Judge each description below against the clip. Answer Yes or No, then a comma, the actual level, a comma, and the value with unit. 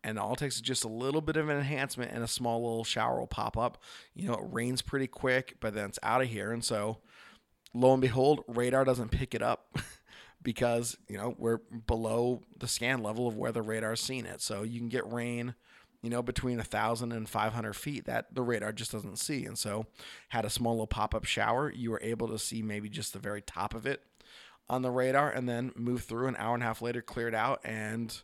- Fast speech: Yes, fast, 235 wpm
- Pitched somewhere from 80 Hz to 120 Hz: Yes, low, 115 Hz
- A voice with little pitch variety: Yes, narrow, 2.2 semitones